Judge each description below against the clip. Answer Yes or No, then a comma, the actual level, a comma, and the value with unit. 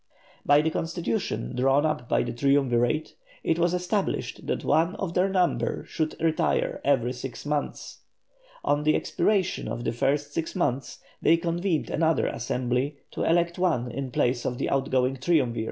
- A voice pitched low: No, medium, 145 Hz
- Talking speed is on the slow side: No, average, 160 wpm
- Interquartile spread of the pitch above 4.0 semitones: Yes, average, 4.8 semitones